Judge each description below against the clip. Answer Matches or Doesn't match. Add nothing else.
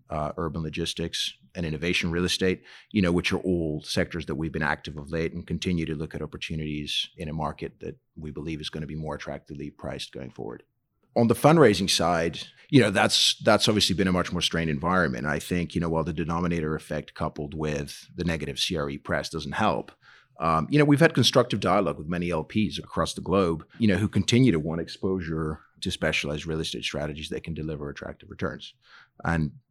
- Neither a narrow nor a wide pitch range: Matches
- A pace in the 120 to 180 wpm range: Doesn't match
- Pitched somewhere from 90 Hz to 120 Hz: Doesn't match